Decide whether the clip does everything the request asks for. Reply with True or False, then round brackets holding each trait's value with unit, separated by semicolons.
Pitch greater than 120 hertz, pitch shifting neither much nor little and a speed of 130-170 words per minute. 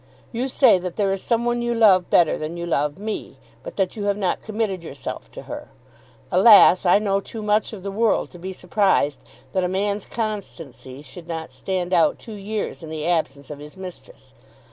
False (190 Hz; 3.9 semitones; 205 wpm)